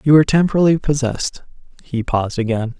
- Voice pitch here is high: No, low, 135 Hz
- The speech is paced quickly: No, average, 150 wpm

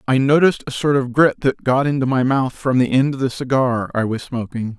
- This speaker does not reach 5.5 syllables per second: No, 5.6 syllables/s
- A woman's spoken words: No, male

